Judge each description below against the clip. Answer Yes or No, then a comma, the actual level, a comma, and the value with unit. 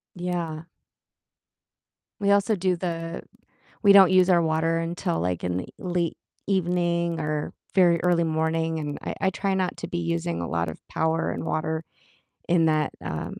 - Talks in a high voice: No, medium, 165 Hz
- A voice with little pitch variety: Yes, narrow, 2.3 semitones